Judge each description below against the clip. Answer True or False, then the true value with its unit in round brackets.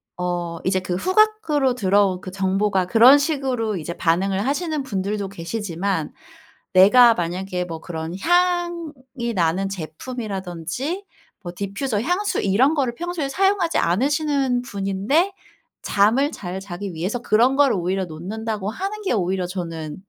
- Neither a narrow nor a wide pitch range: False (6.9 semitones)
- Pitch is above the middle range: True (205 Hz)